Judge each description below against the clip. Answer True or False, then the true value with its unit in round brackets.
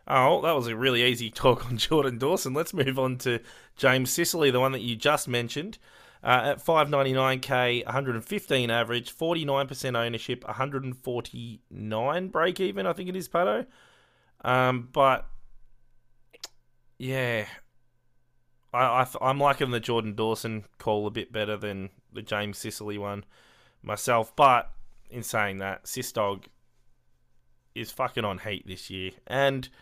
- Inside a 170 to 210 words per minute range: False (140 wpm)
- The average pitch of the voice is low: True (125 Hz)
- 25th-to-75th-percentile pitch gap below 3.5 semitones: True (3.0 semitones)